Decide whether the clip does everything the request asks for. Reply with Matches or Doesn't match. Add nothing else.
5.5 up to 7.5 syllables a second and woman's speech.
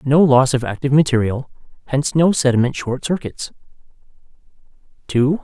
Doesn't match